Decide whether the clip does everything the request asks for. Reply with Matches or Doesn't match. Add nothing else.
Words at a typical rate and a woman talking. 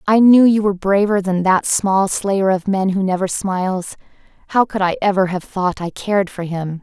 Doesn't match